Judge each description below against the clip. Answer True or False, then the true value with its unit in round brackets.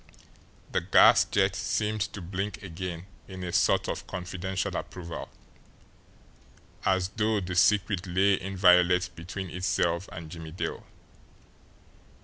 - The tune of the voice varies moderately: False (1.8 semitones)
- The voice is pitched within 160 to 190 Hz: False (90 Hz)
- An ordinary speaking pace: False (120 wpm)